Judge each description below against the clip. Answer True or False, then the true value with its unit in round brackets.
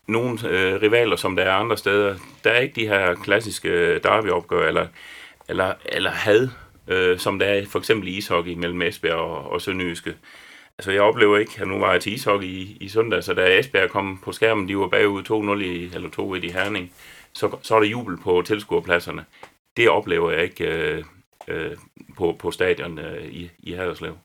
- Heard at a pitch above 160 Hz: False (110 Hz)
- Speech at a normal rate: True (200 wpm)